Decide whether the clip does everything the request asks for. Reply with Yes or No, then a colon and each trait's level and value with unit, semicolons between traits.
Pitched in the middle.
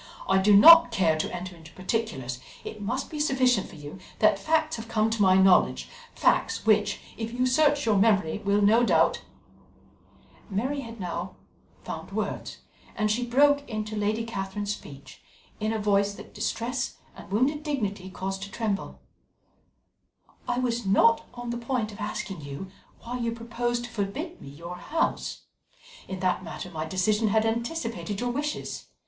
No: high, 215 Hz